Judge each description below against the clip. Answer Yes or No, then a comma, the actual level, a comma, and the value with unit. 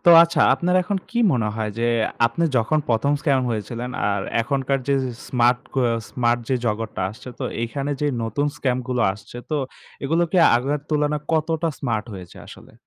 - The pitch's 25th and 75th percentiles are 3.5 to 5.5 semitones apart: Yes, average, 4.5 semitones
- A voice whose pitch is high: No, low, 130 Hz